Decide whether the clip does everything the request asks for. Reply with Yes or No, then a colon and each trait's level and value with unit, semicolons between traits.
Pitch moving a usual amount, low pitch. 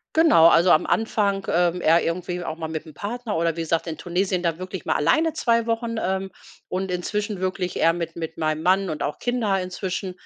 No: average, 3.3 semitones; medium, 180 Hz